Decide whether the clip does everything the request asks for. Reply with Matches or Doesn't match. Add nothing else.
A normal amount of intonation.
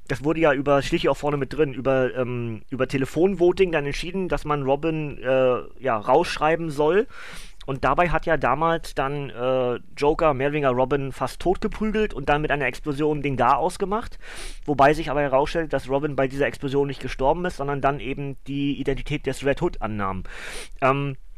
Matches